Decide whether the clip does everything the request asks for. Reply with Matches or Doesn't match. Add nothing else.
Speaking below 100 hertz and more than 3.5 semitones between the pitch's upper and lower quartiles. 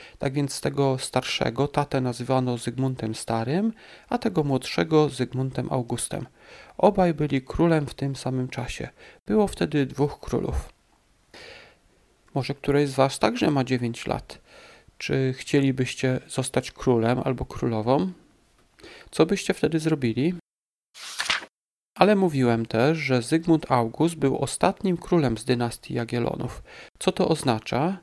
Doesn't match